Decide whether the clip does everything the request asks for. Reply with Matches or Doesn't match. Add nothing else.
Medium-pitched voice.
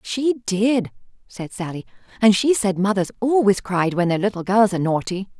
Doesn't match